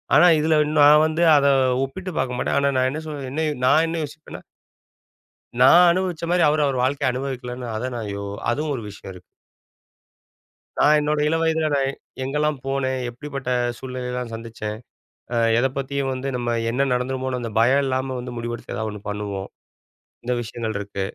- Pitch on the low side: Yes, low, 130 Hz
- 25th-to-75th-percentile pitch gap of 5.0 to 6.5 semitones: No, average, 3.8 semitones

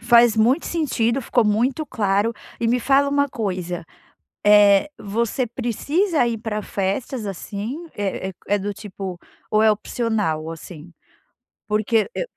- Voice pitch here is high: Yes, high, 220 Hz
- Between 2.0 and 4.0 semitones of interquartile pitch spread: Yes, average, 3.7 semitones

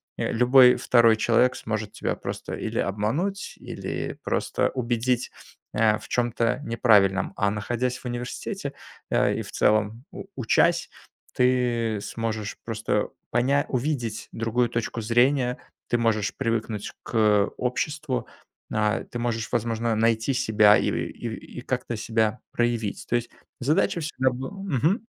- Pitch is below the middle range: Yes, low, 120 Hz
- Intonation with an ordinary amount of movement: No, narrow, 2.3 semitones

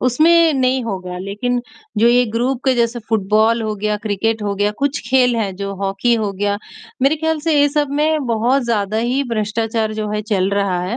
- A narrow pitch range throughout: No, average, 4.0 semitones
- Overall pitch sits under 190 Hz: No, high, 225 Hz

